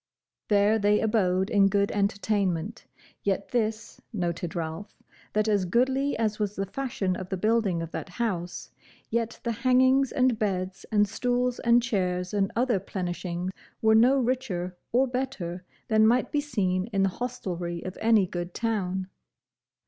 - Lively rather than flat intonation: No, average, 4.2 semitones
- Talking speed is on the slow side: No, average, 155 wpm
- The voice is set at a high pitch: Yes, high, 205 Hz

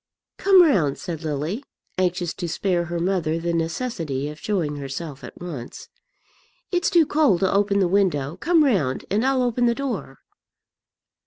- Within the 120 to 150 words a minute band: No, average, 160 wpm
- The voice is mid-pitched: Yes, medium, 180 Hz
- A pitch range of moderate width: No, wide, 7.1 semitones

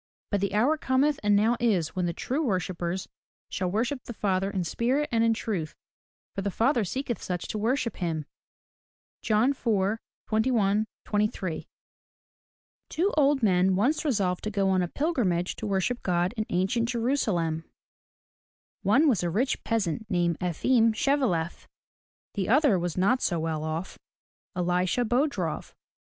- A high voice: Yes, high, 210 Hz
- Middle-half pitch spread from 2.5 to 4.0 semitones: No, average, 5.2 semitones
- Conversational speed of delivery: Yes, average, 160 wpm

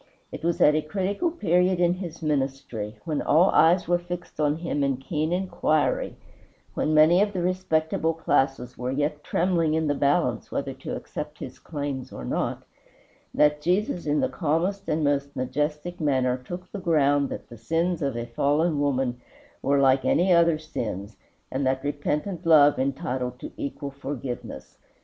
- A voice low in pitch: No, medium, 150 Hz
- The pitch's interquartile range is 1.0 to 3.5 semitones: No, average, 3.9 semitones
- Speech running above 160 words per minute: Yes, average, 170 wpm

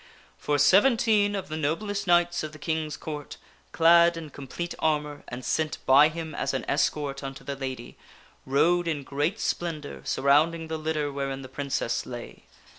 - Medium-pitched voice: Yes, medium, 155 Hz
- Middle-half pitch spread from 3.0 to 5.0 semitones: Yes, average, 3.3 semitones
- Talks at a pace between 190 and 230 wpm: No, average, 170 wpm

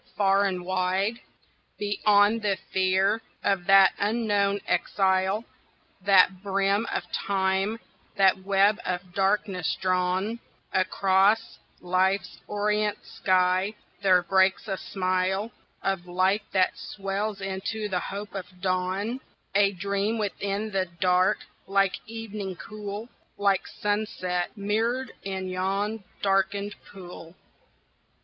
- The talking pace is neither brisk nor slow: No, slow, 110 wpm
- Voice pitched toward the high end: Yes, high, 195 Hz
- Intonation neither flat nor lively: No, narrow, 1.7 semitones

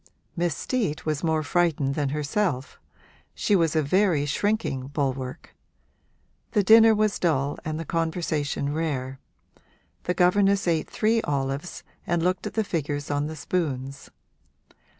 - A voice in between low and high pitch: Yes, medium, 160 Hz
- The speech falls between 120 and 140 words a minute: Yes, slow, 135 wpm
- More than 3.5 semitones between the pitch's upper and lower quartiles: Yes, average, 4.3 semitones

